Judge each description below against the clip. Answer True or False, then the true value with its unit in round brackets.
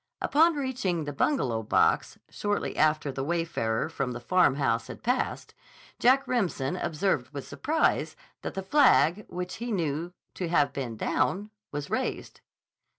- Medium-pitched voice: True (170 Hz)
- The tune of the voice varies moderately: False (7.2 semitones)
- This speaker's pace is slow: False (145 wpm)